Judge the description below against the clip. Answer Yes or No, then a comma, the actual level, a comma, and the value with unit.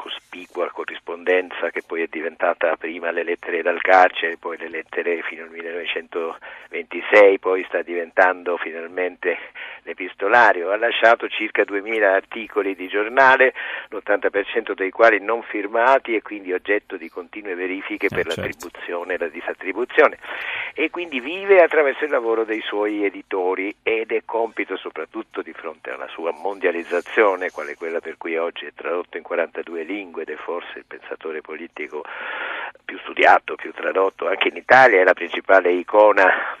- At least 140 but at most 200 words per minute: Yes, average, 150 wpm